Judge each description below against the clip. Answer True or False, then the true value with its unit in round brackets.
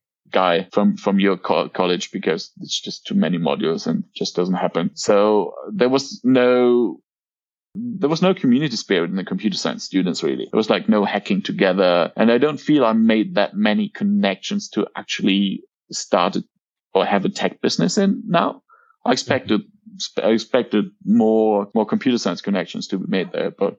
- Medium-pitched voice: True (165 Hz)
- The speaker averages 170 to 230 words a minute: True (175 wpm)